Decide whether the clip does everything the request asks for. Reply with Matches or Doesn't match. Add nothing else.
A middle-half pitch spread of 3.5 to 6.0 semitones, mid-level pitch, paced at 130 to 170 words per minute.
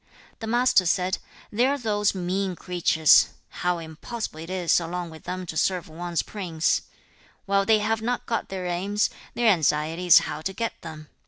Doesn't match